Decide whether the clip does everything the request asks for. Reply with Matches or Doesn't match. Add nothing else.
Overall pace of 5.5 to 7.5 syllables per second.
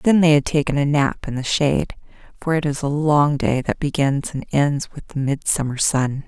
Doesn't match